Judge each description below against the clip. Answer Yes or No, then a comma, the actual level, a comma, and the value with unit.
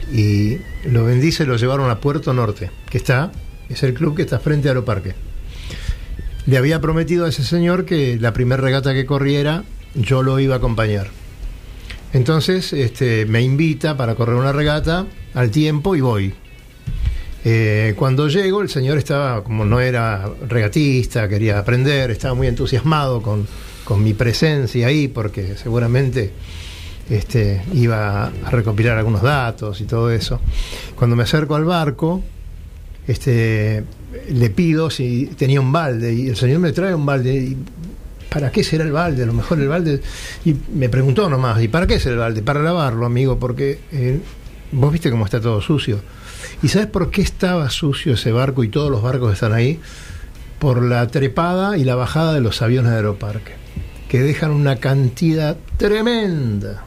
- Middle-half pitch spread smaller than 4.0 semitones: No, average, 4.8 semitones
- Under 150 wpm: No, average, 170 wpm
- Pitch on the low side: Yes, low, 130 Hz